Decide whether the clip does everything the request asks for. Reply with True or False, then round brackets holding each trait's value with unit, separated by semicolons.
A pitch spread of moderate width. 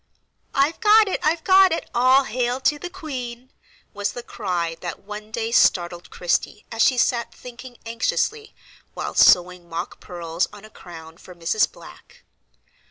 False (6.7 semitones)